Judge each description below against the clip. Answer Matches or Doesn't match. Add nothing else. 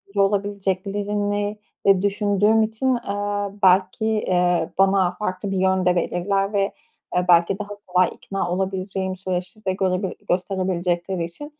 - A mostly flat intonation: Matches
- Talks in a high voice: Matches